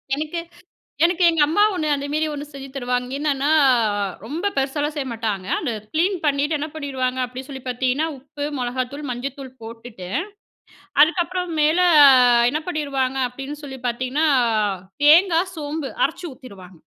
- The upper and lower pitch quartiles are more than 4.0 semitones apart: No, average, 3.4 semitones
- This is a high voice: Yes, very high, 280 Hz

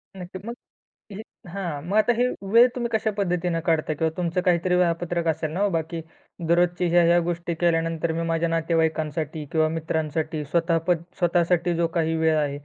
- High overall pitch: No, medium, 170 Hz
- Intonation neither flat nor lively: No, narrow, 1.7 semitones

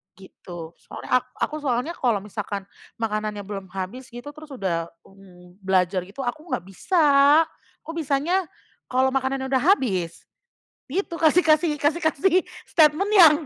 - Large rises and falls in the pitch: Yes, wide, 7.8 semitones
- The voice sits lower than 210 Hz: No, very high, 260 Hz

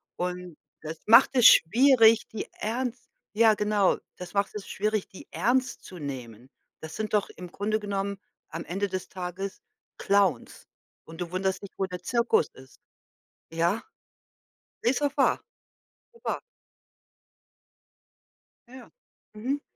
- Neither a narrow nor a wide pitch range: Yes, average, 3.9 semitones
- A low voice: No, high, 200 Hz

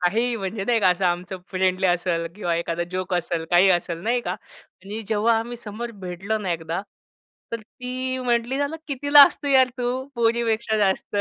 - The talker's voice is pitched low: No, high, 210 Hz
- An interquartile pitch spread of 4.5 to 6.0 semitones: Yes, average, 4.8 semitones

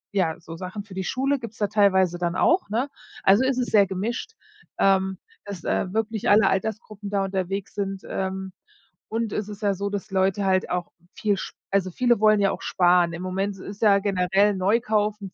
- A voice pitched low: No, high, 200 Hz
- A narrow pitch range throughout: Yes, narrow, 2.1 semitones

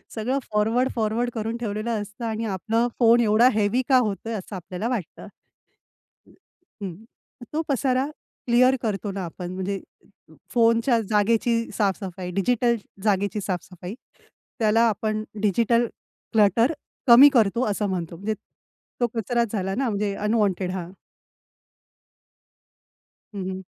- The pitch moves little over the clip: No, average, 3.1 semitones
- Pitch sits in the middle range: No, high, 215 Hz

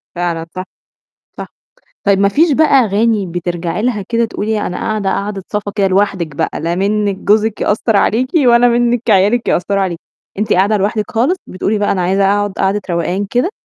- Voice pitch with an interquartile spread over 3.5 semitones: No, average, 2.7 semitones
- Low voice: No, high, 205 Hz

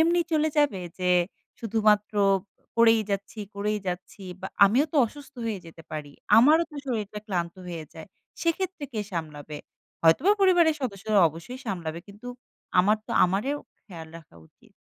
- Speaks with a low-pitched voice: No, high, 210 Hz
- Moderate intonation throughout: No, wide, 7.5 semitones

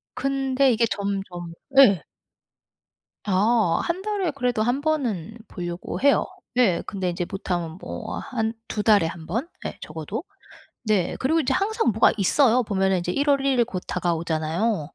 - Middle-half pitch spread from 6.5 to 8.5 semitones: Yes, wide, 7.0 semitones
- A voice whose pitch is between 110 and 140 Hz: No, high, 215 Hz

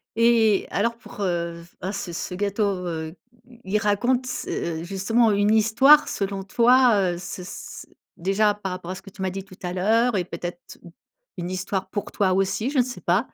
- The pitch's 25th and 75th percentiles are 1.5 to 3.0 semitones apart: No, average, 3.6 semitones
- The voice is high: Yes, high, 200 Hz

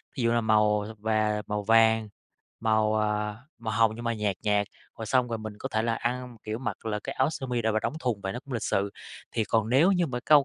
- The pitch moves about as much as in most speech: No, narrow, 2.3 semitones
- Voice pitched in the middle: No, low, 110 Hz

